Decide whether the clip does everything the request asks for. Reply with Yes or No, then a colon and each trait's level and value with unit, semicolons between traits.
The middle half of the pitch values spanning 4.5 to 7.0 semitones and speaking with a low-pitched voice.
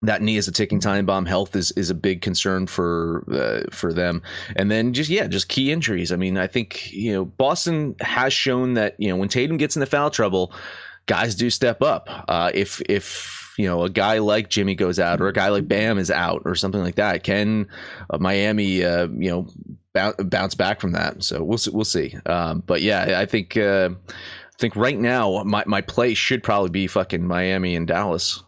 No: average, 3.6 semitones; low, 100 Hz